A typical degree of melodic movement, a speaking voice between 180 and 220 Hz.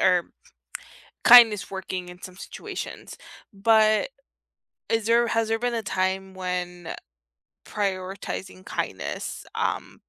Yes: average, 3.5 semitones; high, 190 Hz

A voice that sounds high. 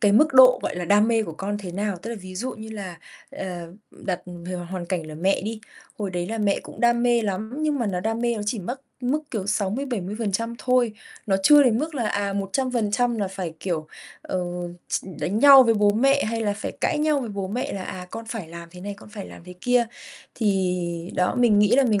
Yes: high, 210 Hz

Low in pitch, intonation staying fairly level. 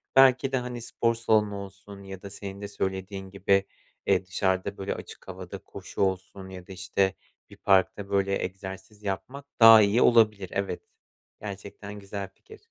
Yes: low, 100 Hz; narrow, 1.8 semitones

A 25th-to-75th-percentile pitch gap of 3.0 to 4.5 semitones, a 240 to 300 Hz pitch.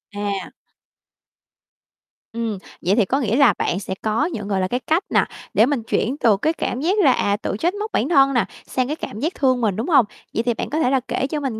No: average, 5.3 semitones; high, 245 Hz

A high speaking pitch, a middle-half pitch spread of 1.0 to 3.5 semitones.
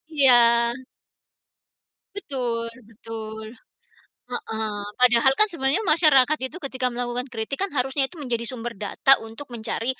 Yes: very high, 250 Hz; average, 3.1 semitones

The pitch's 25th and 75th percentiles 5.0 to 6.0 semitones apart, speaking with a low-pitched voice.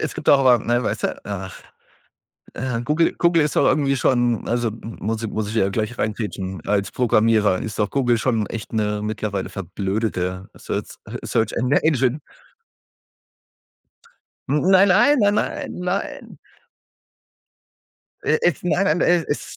Yes: wide, 5.5 semitones; low, 115 Hz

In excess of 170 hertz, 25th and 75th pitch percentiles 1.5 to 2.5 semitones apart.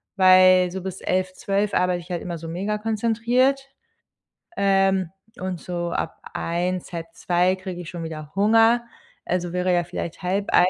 Yes: medium, 185 Hz; narrow, 2.2 semitones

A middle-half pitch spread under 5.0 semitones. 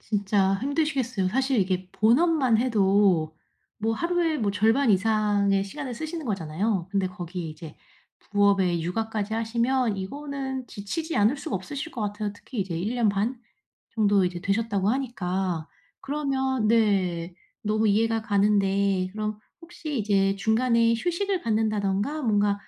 Yes: average, 4.4 semitones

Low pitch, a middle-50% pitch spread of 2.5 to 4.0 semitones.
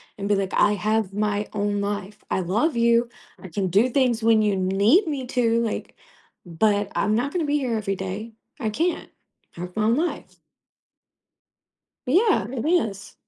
No: high, 215 Hz; average, 3.5 semitones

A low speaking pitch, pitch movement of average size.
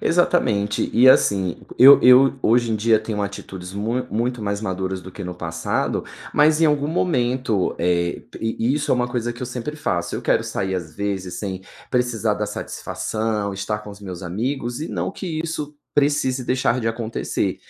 Yes: low, 110 Hz; average, 4.5 semitones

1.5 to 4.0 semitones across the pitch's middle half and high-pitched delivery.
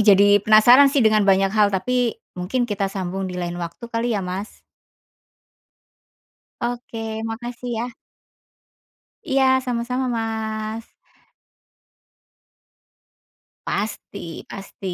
Yes: average, 3.5 semitones; high, 215 Hz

